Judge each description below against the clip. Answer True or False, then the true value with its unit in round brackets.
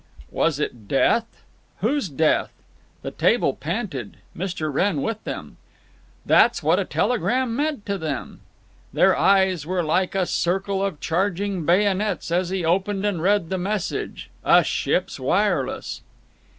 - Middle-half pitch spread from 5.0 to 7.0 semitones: False (3.6 semitones)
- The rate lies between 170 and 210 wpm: False (135 wpm)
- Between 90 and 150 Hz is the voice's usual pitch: False (190 Hz)